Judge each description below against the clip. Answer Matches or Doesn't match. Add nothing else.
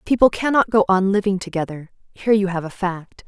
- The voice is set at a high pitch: Matches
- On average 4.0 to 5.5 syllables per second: Doesn't match